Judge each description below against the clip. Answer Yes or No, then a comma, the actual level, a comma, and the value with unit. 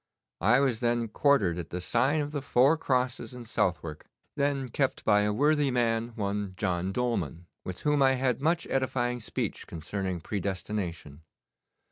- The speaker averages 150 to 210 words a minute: Yes, average, 155 wpm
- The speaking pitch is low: Yes, low, 120 Hz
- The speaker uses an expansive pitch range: Yes, wide, 5.7 semitones